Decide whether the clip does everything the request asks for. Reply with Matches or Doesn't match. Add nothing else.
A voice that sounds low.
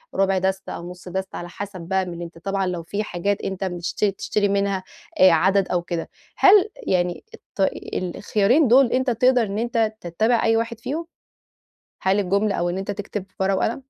Doesn't match